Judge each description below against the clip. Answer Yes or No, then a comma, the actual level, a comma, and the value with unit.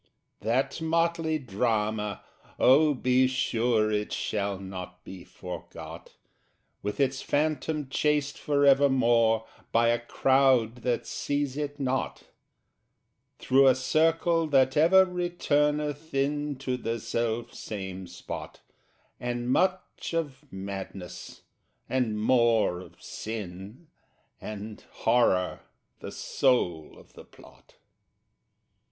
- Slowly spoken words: Yes, slow, 105 wpm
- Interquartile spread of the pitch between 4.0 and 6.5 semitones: Yes, average, 5.3 semitones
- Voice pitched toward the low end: Yes, low, 130 Hz